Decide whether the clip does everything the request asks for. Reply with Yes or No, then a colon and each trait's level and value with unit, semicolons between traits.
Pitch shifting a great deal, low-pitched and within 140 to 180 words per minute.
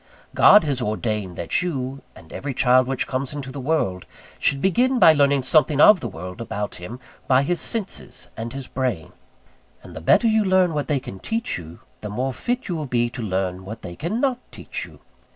No: wide, 6.9 semitones; low, 130 Hz; fast, 205 wpm